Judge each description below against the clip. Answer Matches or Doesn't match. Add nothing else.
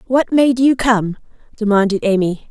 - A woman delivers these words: Matches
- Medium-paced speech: Matches